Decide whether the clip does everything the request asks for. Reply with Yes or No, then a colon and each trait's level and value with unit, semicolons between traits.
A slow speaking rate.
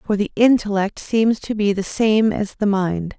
No: fast, 205 wpm